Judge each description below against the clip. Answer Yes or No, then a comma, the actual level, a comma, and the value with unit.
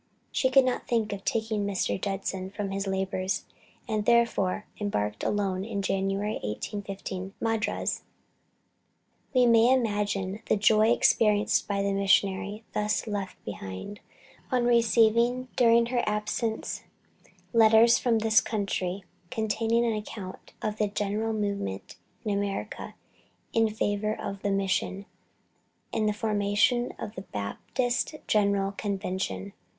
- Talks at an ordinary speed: No, slow, 125 wpm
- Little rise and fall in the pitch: Yes, narrow, 2.3 semitones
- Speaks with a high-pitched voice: Yes, high, 210 Hz